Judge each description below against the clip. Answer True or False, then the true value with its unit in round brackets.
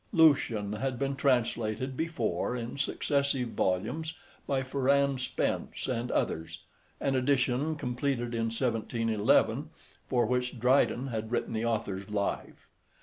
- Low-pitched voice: True (125 Hz)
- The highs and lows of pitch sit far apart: False (3.4 semitones)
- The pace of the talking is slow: True (120 wpm)